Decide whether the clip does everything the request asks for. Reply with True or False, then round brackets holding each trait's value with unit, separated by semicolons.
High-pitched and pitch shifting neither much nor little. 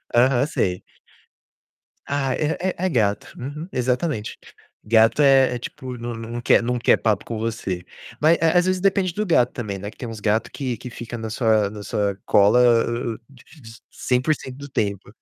False (120 Hz; 4.0 semitones)